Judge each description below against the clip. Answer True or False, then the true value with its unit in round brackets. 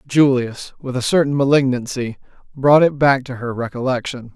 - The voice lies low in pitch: True (130 Hz)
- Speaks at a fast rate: False (150 wpm)